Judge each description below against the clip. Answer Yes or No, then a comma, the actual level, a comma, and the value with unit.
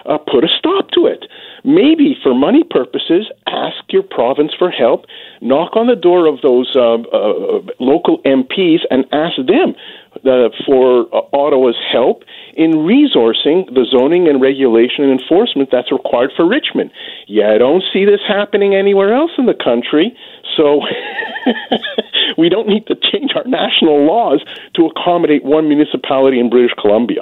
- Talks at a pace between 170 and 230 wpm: No, average, 160 wpm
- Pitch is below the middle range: No, medium, 175 Hz